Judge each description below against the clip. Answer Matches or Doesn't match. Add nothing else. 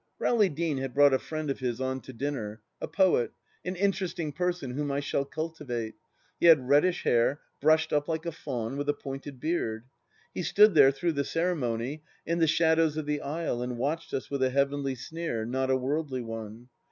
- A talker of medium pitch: Matches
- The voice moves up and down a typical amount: Matches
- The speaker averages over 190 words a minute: Matches